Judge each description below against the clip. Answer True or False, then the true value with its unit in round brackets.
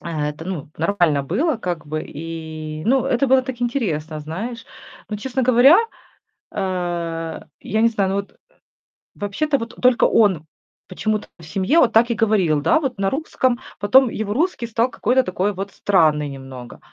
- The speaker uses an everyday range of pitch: False (6.8 semitones)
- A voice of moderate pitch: False (200 Hz)